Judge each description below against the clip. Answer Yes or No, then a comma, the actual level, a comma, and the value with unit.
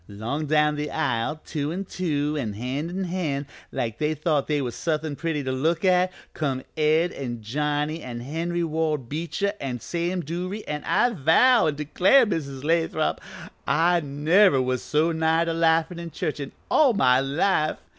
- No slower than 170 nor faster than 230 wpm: Yes, average, 175 wpm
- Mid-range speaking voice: Yes, medium, 155 Hz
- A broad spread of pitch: No, average, 3.2 semitones